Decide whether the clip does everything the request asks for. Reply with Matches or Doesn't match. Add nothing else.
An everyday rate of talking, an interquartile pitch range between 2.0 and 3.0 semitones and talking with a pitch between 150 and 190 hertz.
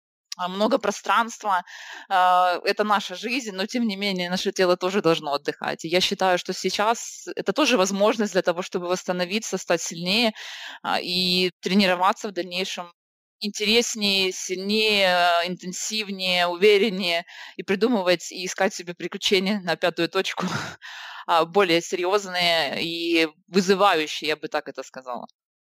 Matches